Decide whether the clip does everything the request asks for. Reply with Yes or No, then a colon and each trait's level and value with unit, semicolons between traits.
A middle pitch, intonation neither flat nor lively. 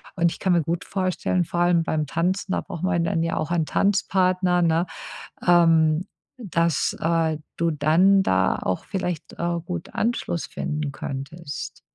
No: medium, 170 Hz; narrow, 2.2 semitones